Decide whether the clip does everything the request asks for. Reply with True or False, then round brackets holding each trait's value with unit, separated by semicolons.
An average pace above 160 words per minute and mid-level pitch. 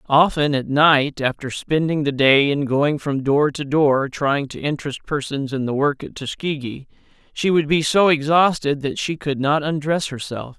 True (185 wpm; 145 Hz)